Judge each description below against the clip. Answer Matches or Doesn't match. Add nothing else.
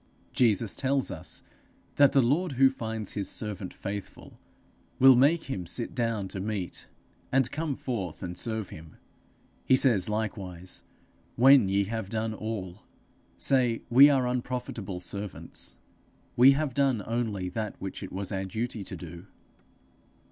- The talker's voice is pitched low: Matches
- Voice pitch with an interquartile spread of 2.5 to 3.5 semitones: Doesn't match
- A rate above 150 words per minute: Doesn't match